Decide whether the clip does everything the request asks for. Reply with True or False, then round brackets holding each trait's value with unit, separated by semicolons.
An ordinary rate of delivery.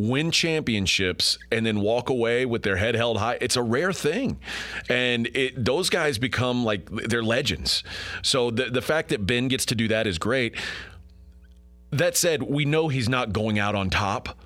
True (185 wpm)